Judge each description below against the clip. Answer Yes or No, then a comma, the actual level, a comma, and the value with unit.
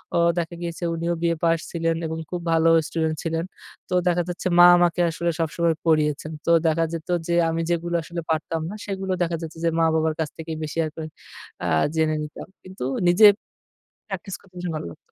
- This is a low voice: No, medium, 165 Hz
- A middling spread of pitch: No, narrow, 1.3 semitones